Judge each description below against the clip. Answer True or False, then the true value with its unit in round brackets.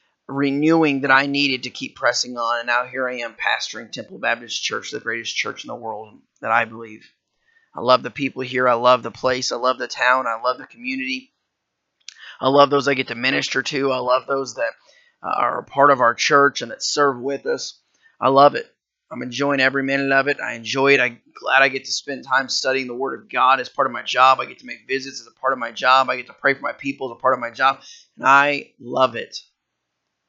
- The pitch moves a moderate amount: False (1.9 semitones)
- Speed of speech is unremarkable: False (245 wpm)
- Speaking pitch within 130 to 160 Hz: True (135 Hz)